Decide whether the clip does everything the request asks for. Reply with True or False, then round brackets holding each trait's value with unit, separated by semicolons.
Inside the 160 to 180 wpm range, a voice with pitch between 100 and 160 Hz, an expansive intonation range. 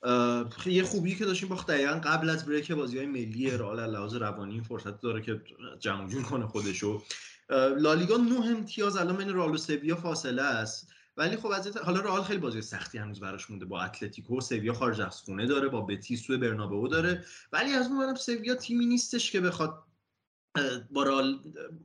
False (190 wpm; 135 Hz; 8.4 semitones)